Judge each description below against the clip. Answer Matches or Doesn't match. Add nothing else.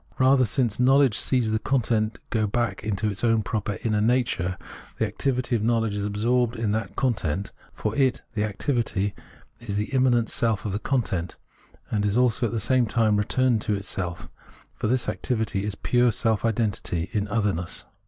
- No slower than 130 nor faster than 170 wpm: Doesn't match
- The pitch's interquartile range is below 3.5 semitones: Matches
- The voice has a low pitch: Matches